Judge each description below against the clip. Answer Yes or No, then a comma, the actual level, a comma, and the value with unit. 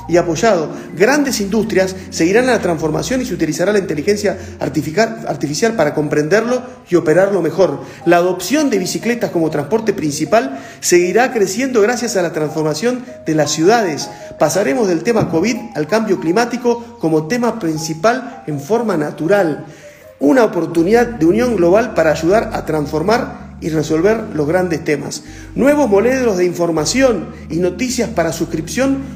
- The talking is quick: No, average, 145 wpm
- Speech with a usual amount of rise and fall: No, wide, 6.8 semitones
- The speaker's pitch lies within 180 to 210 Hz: Yes, high, 190 Hz